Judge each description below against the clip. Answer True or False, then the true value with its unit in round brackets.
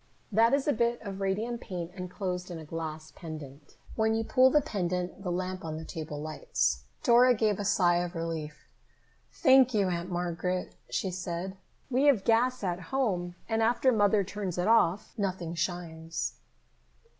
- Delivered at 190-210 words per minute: False (170 wpm)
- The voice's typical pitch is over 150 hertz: True (185 Hz)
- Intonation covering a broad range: False (4.6 semitones)